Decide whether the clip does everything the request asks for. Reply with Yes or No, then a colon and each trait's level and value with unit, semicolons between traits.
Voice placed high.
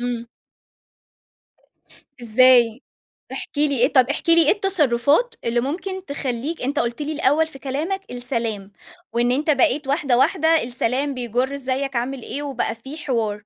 Yes: very high, 270 Hz